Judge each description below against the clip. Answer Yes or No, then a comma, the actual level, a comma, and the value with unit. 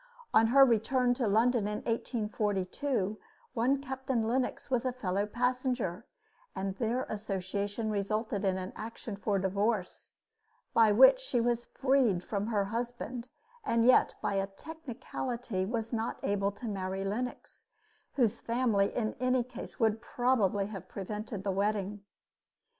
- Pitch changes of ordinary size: Yes, average, 3.6 semitones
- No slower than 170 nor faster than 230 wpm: No, average, 140 wpm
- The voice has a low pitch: No, high, 220 Hz